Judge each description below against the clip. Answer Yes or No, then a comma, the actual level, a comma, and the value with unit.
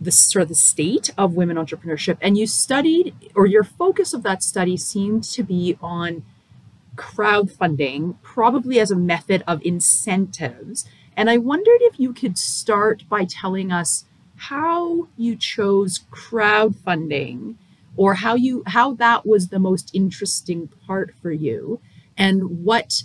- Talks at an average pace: Yes, average, 145 wpm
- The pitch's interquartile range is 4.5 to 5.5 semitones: Yes, average, 4.9 semitones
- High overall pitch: Yes, high, 195 Hz